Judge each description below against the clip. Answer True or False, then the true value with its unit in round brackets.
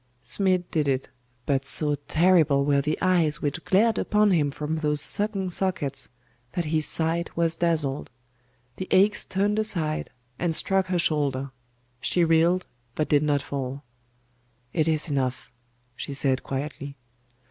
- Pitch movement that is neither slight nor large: True (4.3 semitones)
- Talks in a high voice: False (155 Hz)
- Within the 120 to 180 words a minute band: True (145 wpm)